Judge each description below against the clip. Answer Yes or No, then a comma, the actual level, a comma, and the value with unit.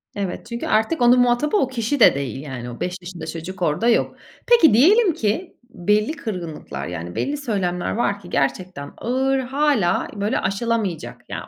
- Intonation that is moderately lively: No, wide, 6.6 semitones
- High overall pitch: Yes, high, 210 Hz